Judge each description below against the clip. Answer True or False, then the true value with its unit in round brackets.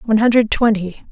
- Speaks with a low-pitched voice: False (220 Hz)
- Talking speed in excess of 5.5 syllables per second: True (5.8 syllables/s)